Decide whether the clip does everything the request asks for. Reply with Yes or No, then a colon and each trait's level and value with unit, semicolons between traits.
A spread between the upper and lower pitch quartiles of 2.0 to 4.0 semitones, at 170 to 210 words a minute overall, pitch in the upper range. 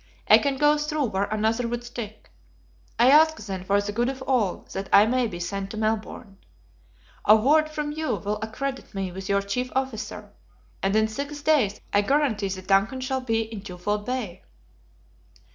No: average, 4.8 semitones; average, 180 wpm; high, 220 Hz